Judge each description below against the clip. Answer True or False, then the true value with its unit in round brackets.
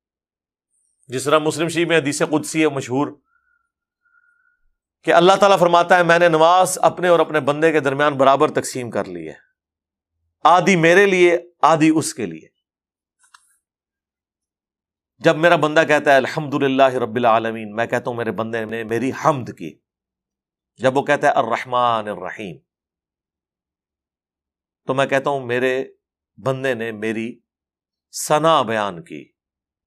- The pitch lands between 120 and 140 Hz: True (135 Hz)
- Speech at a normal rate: True (140 wpm)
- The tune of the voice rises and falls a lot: True (6.6 semitones)